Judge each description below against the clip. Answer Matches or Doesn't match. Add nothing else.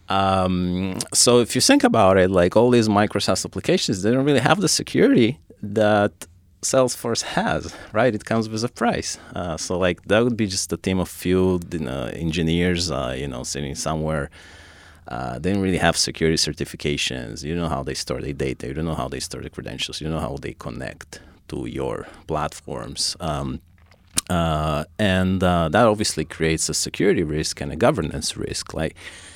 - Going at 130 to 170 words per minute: Doesn't match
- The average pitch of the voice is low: Matches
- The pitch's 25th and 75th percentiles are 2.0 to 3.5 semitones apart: Doesn't match